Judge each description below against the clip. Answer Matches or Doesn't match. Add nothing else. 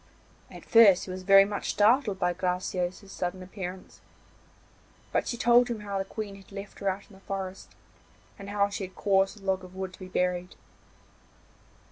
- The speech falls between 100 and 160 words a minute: Doesn't match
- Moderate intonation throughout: Doesn't match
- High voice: Matches